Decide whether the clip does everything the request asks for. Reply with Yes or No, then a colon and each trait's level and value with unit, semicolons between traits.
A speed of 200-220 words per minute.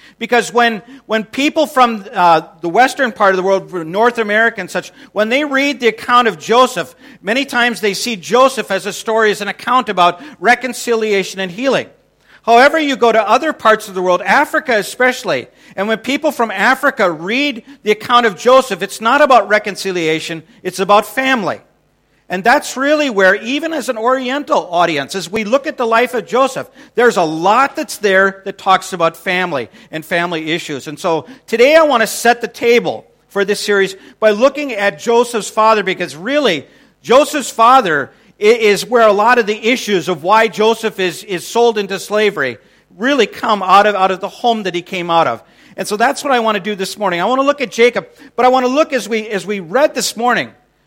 Yes: fast, 205 wpm